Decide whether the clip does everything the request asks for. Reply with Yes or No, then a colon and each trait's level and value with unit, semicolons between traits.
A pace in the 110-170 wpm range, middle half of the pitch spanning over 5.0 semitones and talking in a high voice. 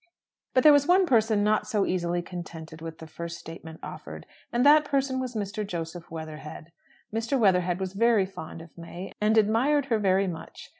No: average, 185 wpm; wide, 5.6 semitones; high, 195 Hz